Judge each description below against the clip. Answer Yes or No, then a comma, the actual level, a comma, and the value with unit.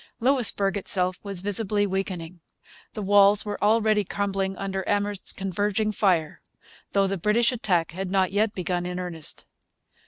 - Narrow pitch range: Yes, narrow, 2.0 semitones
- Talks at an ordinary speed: Yes, average, 145 wpm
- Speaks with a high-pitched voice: Yes, high, 195 Hz